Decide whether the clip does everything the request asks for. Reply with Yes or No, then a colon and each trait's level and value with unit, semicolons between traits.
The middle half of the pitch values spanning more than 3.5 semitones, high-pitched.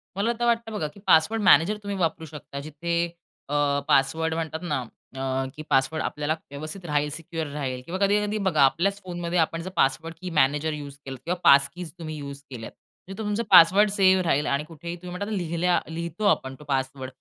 No: average, 4.1 semitones; medium, 160 Hz